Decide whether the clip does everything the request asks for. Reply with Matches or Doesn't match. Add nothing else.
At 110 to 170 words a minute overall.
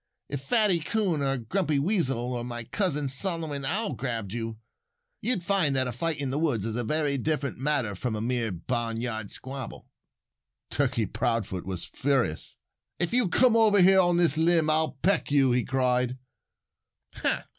Matches